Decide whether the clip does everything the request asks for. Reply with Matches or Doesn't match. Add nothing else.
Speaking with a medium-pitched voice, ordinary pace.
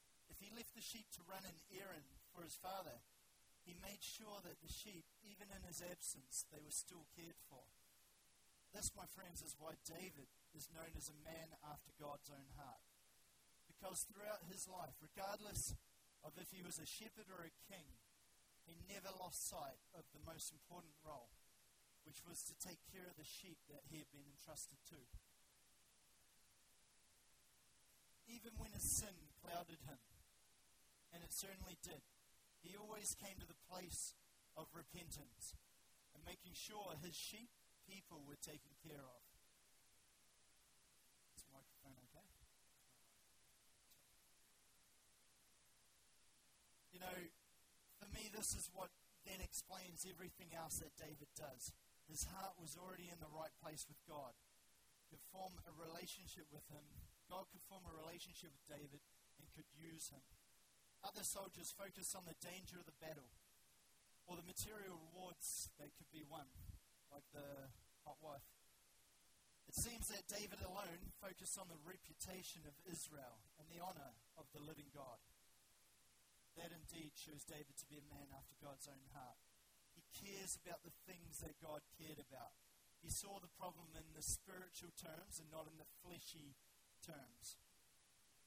Matches